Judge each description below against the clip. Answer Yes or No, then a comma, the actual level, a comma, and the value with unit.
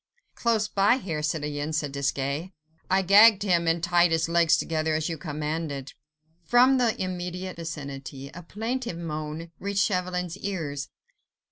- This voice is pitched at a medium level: Yes, medium, 170 Hz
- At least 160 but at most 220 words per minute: No, average, 140 wpm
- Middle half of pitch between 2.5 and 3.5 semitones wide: No, average, 4.0 semitones